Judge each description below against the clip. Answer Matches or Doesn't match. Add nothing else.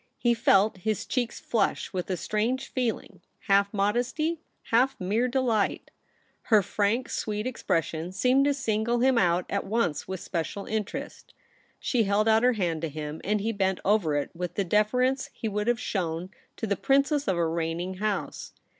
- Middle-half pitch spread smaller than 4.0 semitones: Doesn't match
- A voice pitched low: Doesn't match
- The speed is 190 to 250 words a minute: Doesn't match